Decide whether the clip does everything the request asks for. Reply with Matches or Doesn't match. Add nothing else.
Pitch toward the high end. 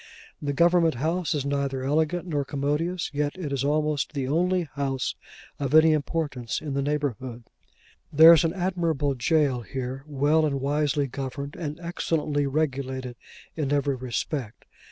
Doesn't match